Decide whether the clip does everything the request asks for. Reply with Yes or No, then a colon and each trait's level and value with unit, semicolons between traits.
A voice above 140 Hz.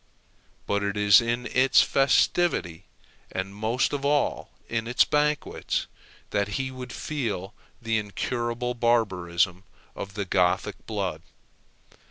No: low, 115 Hz